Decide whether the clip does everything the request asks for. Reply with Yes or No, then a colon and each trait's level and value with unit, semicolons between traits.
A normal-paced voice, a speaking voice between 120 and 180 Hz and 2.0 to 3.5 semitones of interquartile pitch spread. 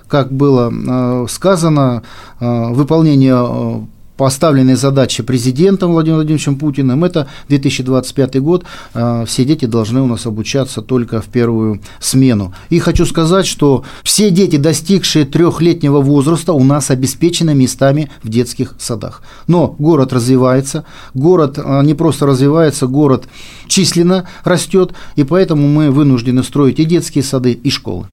No: average, 125 wpm; medium, 140 Hz; average, 4.2 semitones